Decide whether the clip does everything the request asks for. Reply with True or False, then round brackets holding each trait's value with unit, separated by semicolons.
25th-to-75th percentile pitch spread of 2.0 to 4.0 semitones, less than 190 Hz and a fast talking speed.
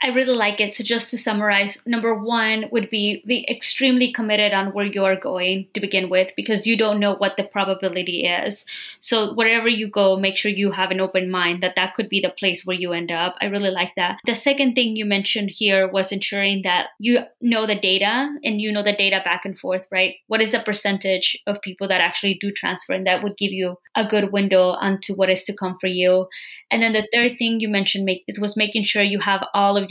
False (2.5 semitones; 200 Hz; 235 wpm)